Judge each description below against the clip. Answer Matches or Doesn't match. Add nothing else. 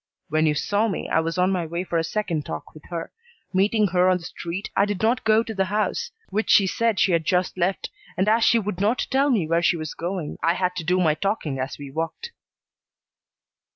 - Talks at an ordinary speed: Doesn't match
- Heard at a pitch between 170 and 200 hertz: Matches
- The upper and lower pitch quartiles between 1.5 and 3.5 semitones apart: Doesn't match